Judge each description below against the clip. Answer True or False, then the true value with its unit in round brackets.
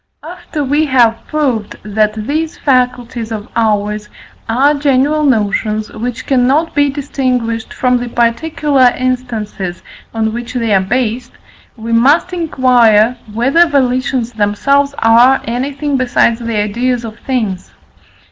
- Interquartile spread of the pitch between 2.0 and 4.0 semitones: True (3.7 semitones)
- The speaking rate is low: True (125 wpm)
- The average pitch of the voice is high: True (245 Hz)